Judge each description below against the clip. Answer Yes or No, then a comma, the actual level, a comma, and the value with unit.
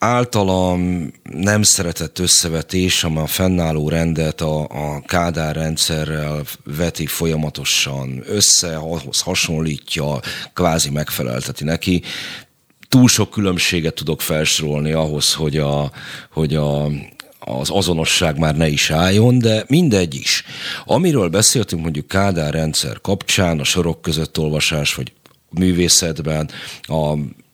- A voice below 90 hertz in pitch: Yes, very low, 80 Hz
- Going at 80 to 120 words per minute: Yes, average, 115 wpm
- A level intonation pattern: No, average, 3.0 semitones